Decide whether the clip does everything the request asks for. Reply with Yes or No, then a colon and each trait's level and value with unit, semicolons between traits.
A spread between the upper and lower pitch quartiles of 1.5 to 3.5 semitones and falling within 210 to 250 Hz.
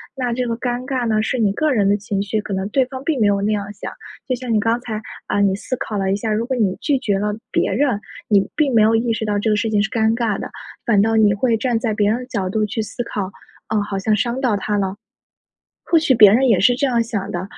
Yes: average, 3.1 semitones; high, 220 Hz